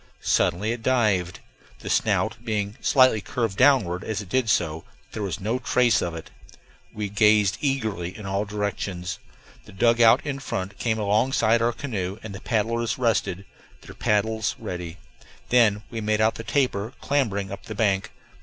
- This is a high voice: No, low, 110 Hz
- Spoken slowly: No, average, 165 wpm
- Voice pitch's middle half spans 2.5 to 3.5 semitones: Yes, average, 3.1 semitones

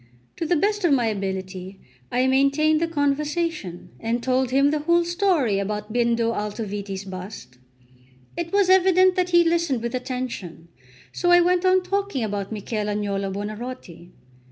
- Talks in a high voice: Yes, very high, 255 Hz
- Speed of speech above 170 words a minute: No, average, 155 wpm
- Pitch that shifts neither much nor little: No, wide, 8.7 semitones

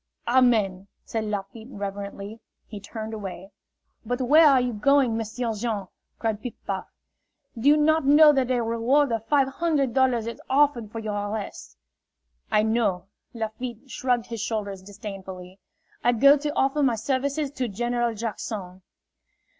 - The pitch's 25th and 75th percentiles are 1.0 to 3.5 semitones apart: No, average, 4.0 semitones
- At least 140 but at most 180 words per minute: Yes, average, 150 wpm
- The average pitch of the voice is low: No, high, 230 Hz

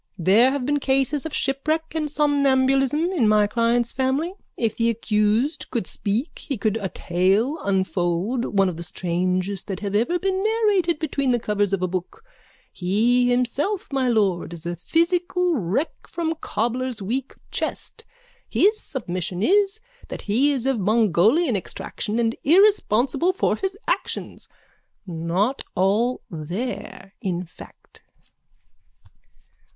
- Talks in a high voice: Yes, high, 240 Hz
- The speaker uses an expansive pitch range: Yes, wide, 7.0 semitones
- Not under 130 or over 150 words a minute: Yes, slow, 135 wpm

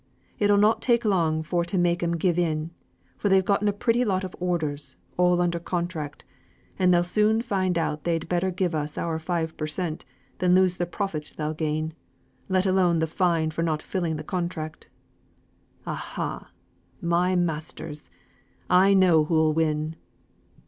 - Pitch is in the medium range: Yes, medium, 175 Hz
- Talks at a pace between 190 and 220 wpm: No, average, 165 wpm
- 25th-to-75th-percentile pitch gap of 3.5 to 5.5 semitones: No, average, 2.8 semitones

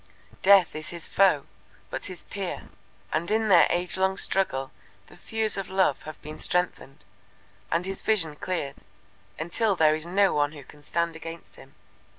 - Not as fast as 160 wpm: No, average, 165 wpm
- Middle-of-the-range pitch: Yes, medium, 170 Hz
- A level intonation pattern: No, average, 3.7 semitones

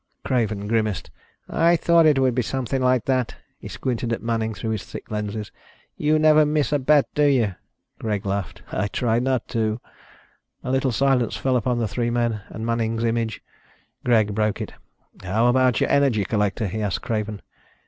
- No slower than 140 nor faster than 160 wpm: No, average, 180 wpm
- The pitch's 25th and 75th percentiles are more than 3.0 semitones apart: Yes, average, 3.4 semitones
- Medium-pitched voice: No, low, 115 Hz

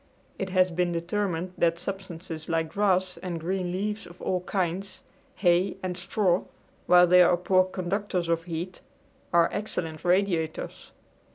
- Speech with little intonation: Yes, narrow, 1.9 semitones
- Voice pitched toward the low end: No, medium, 180 Hz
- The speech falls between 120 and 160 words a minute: Yes, average, 145 wpm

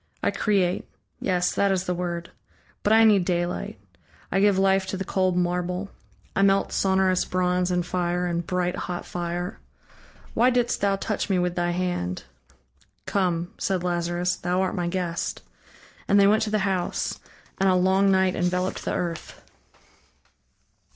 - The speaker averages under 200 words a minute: Yes, average, 160 wpm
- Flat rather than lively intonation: Yes, narrow, 1.6 semitones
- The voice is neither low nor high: Yes, medium, 180 Hz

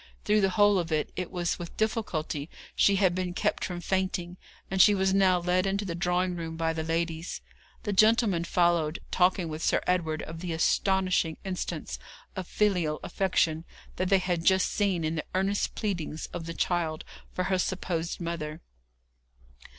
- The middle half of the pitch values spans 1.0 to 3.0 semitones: Yes, narrow, 2.5 semitones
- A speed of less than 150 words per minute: No, average, 170 wpm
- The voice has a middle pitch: Yes, medium, 180 Hz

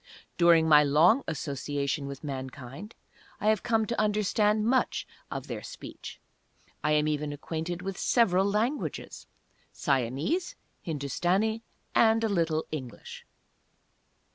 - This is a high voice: No, medium, 170 Hz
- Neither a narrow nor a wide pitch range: No, wide, 6.8 semitones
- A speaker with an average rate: No, slow, 115 wpm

